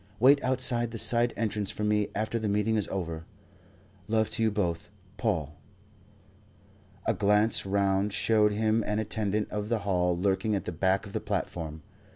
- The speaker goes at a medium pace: Yes, average, 170 wpm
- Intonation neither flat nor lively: No, narrow, 2.2 semitones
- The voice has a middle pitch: No, low, 105 Hz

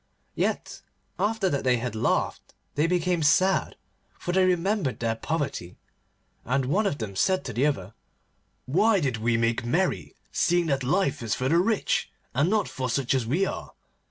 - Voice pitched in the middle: Yes, medium, 145 Hz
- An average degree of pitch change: No, wide, 7.0 semitones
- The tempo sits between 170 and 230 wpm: Yes, average, 175 wpm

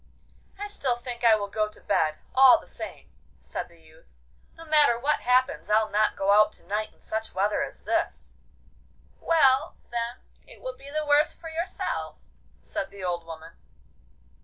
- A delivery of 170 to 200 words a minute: Yes, average, 175 wpm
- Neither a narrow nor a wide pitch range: No, wide, 6.0 semitones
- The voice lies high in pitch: Yes, high, 230 Hz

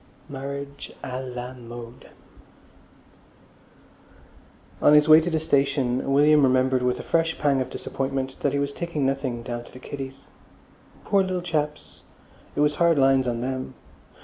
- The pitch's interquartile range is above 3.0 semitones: No, narrow, 2.6 semitones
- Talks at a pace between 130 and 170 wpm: Yes, average, 150 wpm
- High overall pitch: No, low, 135 Hz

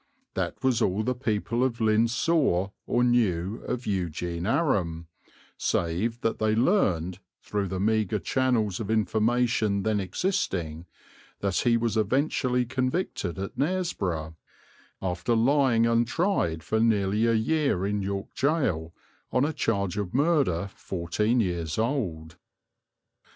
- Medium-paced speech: No, slow, 130 wpm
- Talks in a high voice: No, low, 110 Hz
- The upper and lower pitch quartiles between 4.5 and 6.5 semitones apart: Yes, average, 4.9 semitones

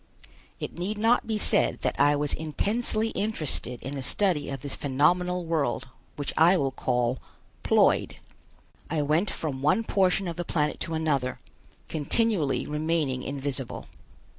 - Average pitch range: Yes, average, 4.6 semitones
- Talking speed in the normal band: Yes, average, 145 wpm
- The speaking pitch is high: No, medium, 155 Hz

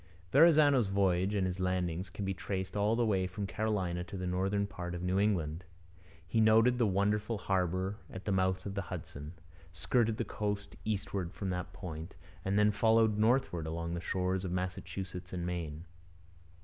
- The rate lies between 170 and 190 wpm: Yes, average, 175 wpm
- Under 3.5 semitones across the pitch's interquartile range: Yes, narrow, 2.6 semitones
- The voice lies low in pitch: Yes, very low, 95 Hz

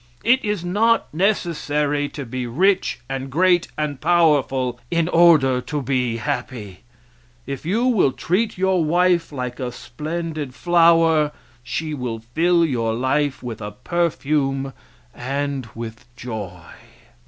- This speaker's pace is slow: Yes, slow, 130 wpm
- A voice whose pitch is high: No, medium, 145 Hz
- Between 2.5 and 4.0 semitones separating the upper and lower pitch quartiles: No, wide, 5.4 semitones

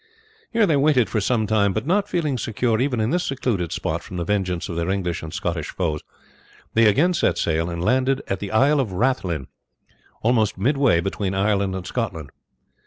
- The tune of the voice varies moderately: No, wide, 6.5 semitones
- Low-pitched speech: Yes, low, 105 Hz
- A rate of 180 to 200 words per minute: Yes, average, 190 wpm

